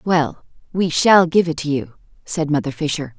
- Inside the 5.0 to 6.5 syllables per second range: No, 4.7 syllables/s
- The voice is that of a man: No, female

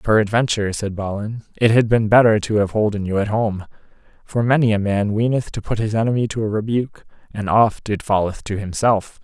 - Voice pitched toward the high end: No, low, 105 Hz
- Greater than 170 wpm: Yes, average, 200 wpm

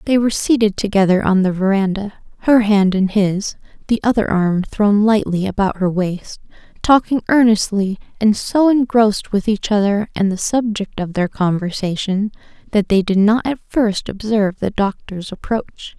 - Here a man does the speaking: No, female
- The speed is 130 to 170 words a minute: Yes, average, 160 wpm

